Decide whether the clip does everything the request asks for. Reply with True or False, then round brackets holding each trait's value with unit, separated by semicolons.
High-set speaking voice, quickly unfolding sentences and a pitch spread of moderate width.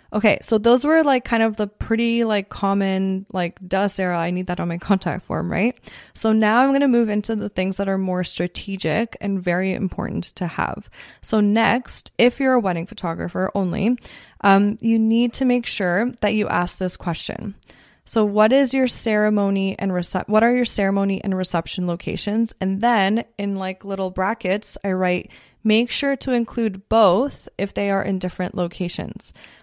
False (200 Hz; 185 wpm; 3.3 semitones)